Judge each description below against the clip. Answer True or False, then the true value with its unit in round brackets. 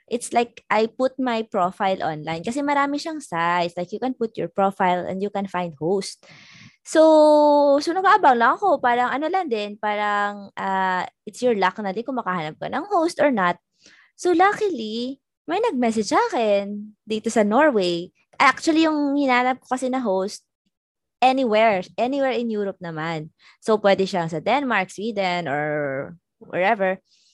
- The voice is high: True (220 Hz)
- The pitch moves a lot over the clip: True (5.7 semitones)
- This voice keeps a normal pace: False (160 wpm)